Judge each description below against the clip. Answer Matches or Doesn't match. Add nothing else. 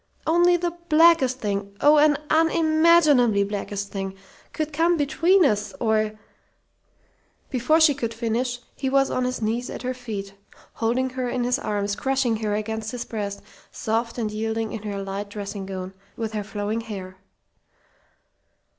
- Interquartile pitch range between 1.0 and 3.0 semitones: Doesn't match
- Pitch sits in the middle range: Doesn't match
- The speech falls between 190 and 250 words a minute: Doesn't match